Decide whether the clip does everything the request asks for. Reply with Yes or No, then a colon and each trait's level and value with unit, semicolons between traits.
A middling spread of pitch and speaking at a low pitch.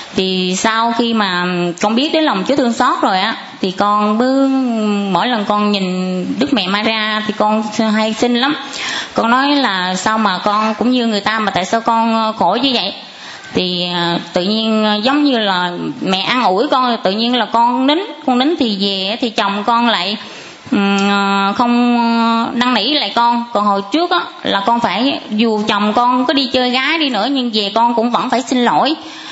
No: average, 3.6 semitones; high, 230 Hz